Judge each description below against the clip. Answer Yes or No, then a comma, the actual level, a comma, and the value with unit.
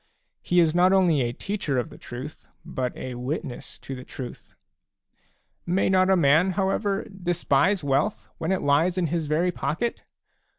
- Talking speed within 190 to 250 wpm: No, average, 170 wpm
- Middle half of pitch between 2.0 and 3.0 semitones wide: No, average, 5.1 semitones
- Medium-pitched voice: Yes, medium, 170 Hz